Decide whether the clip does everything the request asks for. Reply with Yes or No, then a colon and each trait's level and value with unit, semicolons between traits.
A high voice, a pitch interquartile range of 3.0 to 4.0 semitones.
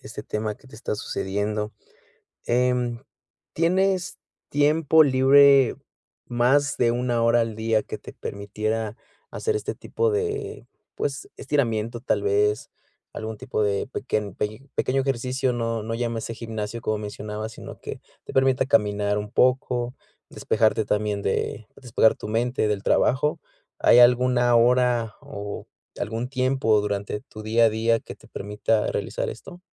No: low, 115 Hz; average, 3.5 semitones